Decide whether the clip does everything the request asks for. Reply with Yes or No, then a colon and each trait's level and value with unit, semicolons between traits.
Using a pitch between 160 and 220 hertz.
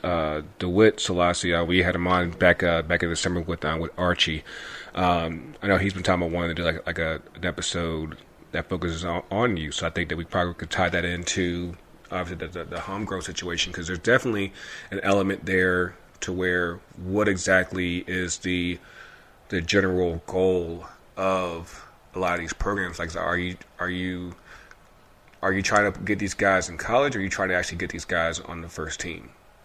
No: very low, 90 Hz